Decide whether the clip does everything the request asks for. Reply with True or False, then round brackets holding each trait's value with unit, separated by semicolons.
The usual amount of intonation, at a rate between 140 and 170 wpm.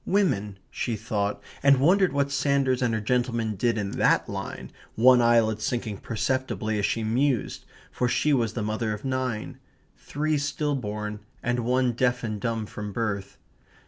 True (3.4 semitones; 165 wpm)